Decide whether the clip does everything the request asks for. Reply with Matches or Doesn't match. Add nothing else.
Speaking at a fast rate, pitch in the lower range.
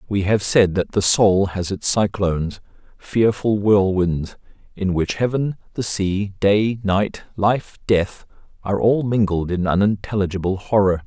Doesn't match